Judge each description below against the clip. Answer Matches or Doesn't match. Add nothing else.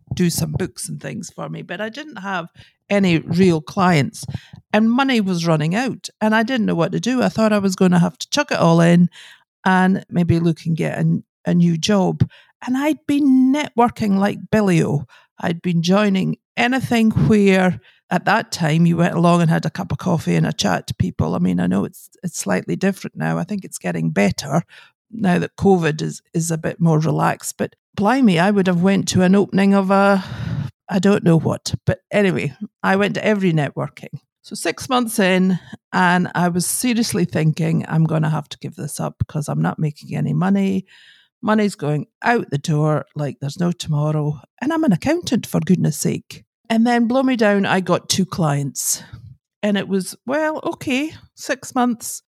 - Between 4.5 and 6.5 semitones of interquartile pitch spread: Matches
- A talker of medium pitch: Matches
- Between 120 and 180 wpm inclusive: Doesn't match